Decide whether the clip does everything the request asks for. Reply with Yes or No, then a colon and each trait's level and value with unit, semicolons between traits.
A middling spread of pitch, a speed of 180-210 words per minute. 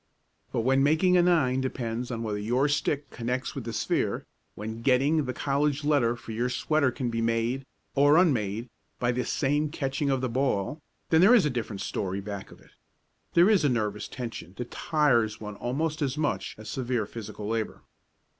Yes: average, 4.2 semitones; average, 190 wpm